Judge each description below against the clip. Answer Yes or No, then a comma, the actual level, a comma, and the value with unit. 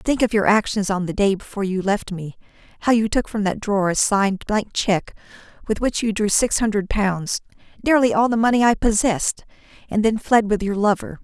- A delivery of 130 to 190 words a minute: No, fast, 205 wpm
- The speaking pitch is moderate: No, high, 210 Hz